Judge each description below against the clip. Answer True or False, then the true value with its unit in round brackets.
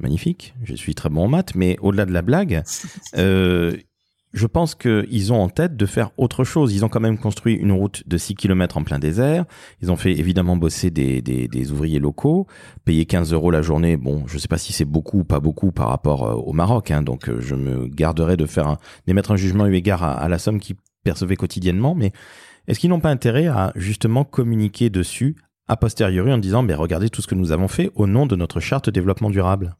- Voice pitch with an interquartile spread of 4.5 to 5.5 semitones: True (5.0 semitones)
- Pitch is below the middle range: True (95 Hz)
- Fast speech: True (230 wpm)